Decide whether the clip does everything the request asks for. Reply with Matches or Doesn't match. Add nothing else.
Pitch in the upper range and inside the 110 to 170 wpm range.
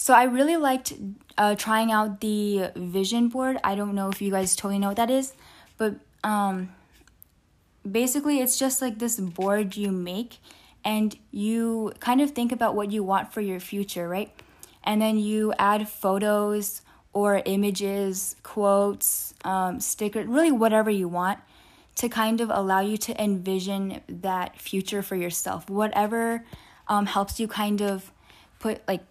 Matches